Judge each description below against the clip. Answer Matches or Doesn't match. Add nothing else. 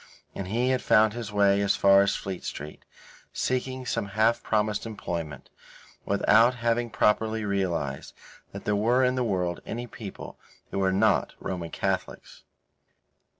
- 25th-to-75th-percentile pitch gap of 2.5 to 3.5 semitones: Matches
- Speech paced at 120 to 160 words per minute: Matches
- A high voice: Doesn't match